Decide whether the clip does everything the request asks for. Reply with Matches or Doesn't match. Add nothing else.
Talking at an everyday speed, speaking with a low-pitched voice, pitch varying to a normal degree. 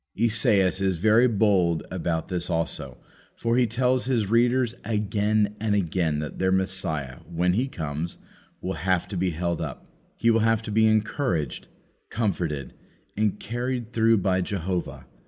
Matches